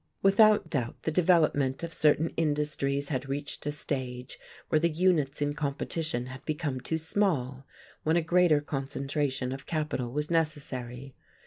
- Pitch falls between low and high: Yes, medium, 145 Hz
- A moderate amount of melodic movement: Yes, average, 3.1 semitones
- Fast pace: No, average, 145 wpm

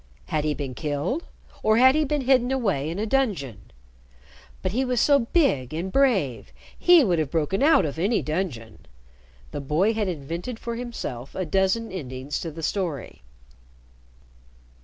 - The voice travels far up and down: Yes, wide, 8.7 semitones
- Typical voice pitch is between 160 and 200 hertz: Yes, medium, 185 Hz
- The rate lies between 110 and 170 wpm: Yes, average, 160 wpm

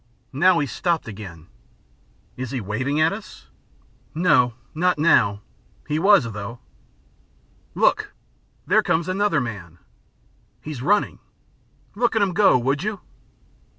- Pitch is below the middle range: No, medium, 150 Hz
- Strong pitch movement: Yes, wide, 7.8 semitones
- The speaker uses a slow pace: Yes, slow, 120 wpm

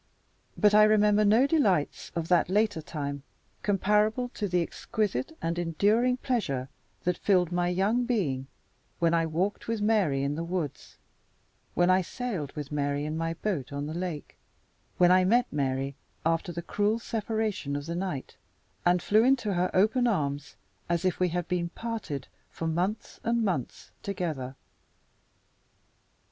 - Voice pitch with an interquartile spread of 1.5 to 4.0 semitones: No, average, 5.2 semitones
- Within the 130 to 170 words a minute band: Yes, average, 155 wpm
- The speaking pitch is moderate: Yes, medium, 180 Hz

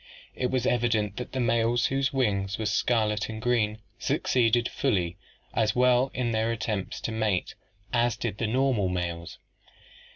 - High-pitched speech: No, low, 115 Hz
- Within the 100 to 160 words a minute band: Yes, average, 155 wpm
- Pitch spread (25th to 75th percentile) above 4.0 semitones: No, average, 2.7 semitones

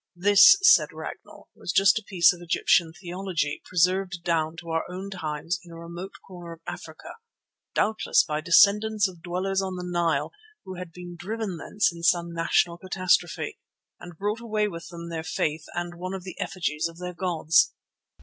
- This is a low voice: No, medium, 175 Hz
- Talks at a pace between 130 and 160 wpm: No, average, 180 wpm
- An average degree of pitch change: No, narrow, 2.3 semitones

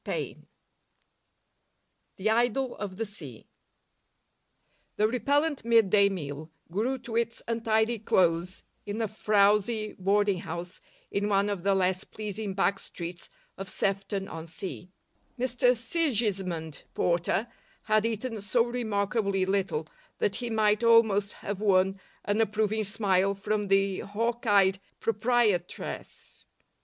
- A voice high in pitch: Yes, high, 205 Hz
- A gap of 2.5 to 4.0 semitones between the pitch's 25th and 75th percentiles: Yes, average, 2.9 semitones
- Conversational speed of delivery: No, slow, 120 wpm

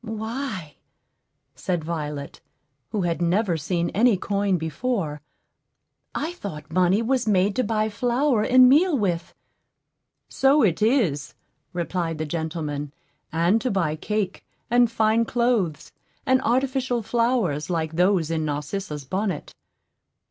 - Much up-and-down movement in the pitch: Yes, wide, 6.5 semitones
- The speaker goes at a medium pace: No, slow, 125 wpm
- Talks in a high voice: Yes, high, 195 Hz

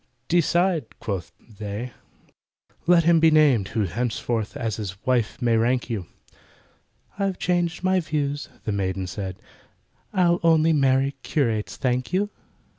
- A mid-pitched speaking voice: No, low, 130 Hz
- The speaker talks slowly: Yes, slow, 130 wpm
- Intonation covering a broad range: Yes, wide, 7.3 semitones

